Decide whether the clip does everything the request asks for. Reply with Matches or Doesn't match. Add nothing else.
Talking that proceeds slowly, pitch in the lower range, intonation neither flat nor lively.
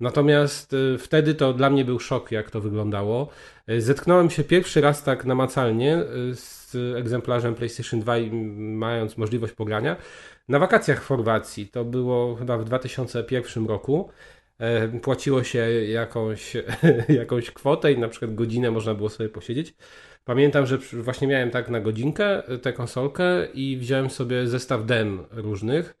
Doesn't match